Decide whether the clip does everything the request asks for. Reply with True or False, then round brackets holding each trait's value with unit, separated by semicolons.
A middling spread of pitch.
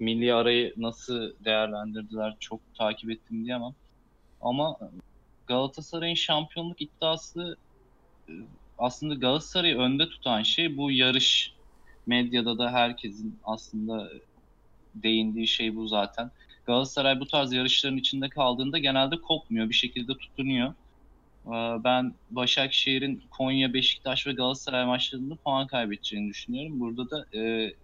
True (3.2 semitones)